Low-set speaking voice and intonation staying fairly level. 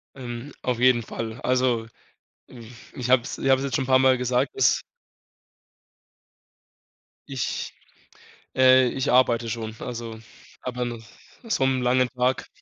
Yes: low, 125 Hz; narrow, 1.7 semitones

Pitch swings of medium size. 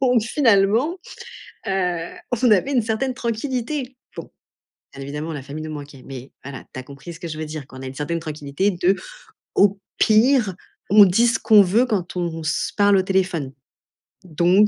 No: wide, 6.3 semitones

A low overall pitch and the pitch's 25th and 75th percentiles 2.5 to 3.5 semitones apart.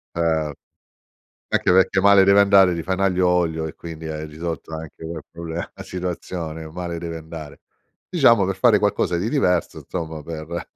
Yes: very low, 85 Hz; average, 2.8 semitones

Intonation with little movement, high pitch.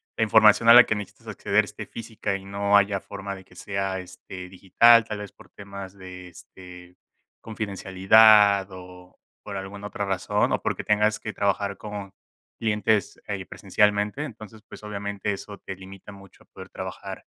No: narrow, 1.7 semitones; low, 100 Hz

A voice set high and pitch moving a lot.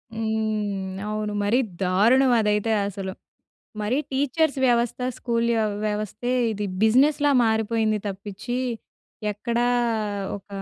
No: high, 220 Hz; narrow, 2.6 semitones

